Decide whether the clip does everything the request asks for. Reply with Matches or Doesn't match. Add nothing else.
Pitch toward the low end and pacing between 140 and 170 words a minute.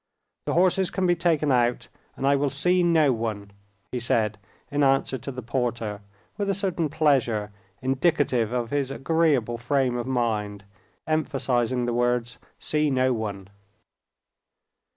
Matches